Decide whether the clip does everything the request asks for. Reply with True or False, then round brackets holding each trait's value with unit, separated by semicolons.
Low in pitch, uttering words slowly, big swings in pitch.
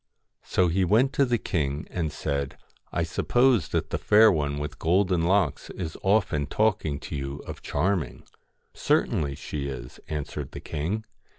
False (80 Hz; 170 wpm; 5.7 semitones)